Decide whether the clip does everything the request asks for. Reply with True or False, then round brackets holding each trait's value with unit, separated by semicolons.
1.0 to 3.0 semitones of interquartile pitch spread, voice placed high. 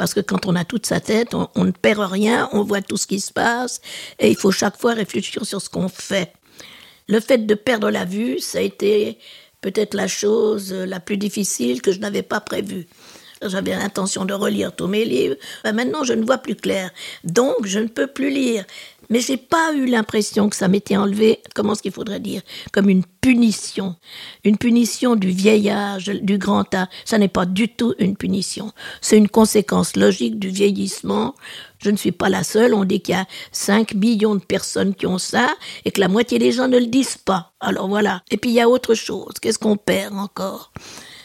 True (2.7 semitones; 205 Hz)